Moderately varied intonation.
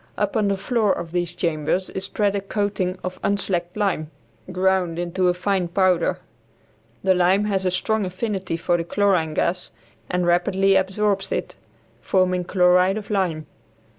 No: narrow, 2.0 semitones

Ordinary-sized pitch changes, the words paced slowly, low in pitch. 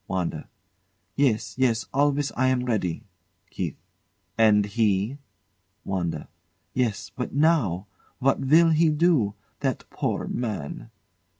No: wide, 5.8 semitones; slow, 110 wpm; low, 120 Hz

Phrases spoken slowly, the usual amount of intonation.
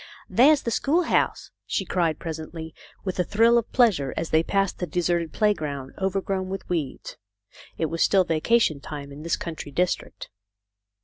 No: average, 160 wpm; average, 4.0 semitones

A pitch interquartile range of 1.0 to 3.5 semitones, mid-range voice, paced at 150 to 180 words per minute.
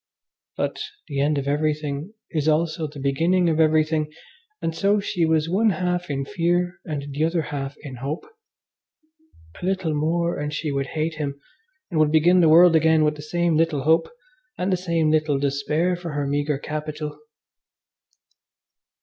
Yes: narrow, 2.4 semitones; medium, 155 Hz; average, 165 wpm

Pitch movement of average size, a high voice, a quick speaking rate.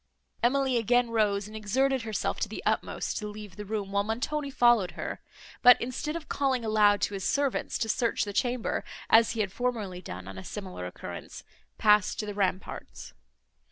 No: average, 3.5 semitones; high, 220 Hz; average, 185 wpm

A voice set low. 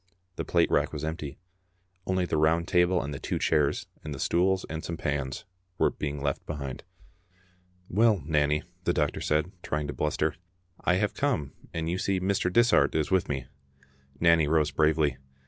Yes: very low, 80 Hz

